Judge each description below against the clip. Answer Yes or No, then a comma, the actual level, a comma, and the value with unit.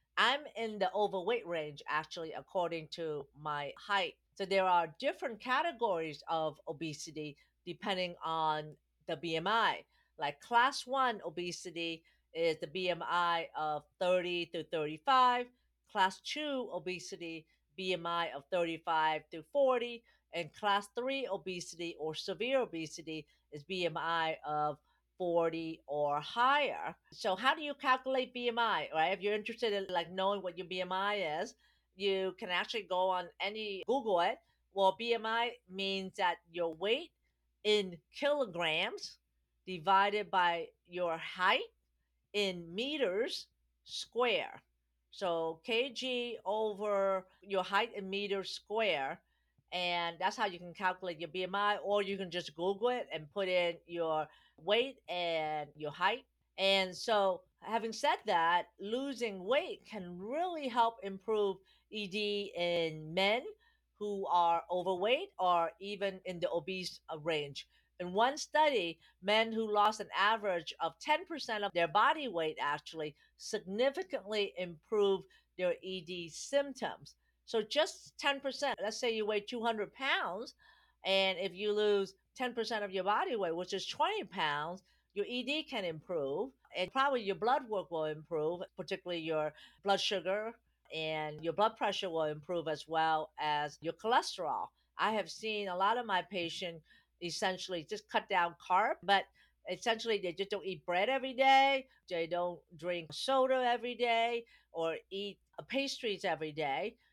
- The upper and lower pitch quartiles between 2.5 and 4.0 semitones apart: No, average, 4.9 semitones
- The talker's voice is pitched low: No, high, 190 Hz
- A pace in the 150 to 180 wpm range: No, average, 140 wpm